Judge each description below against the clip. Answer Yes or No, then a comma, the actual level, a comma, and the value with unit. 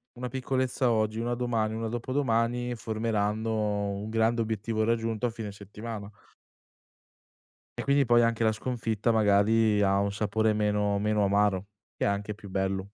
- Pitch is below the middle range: Yes, low, 110 Hz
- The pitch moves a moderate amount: No, narrow, 2.0 semitones